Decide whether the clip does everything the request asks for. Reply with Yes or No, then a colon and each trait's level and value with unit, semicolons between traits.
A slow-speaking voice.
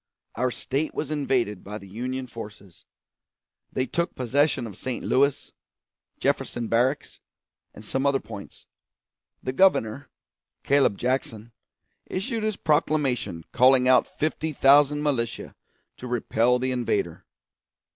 Yes: slow, 120 wpm